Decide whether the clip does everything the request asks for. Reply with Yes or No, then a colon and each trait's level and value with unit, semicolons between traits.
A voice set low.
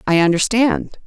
No: high, 200 Hz